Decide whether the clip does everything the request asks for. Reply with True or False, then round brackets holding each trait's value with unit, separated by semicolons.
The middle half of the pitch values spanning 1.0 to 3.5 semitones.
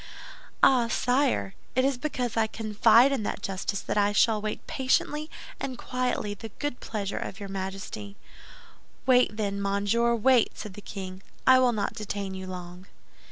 False (4.0 semitones)